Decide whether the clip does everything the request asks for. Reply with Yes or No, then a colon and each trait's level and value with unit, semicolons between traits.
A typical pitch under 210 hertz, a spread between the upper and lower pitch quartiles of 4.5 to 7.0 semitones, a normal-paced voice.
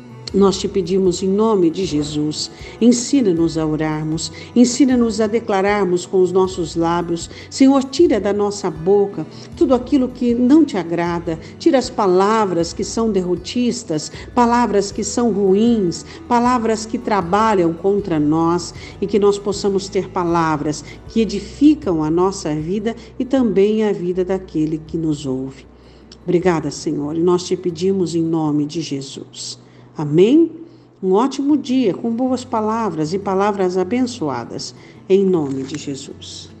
Yes: high, 190 Hz; wide, 5.6 semitones; average, 140 wpm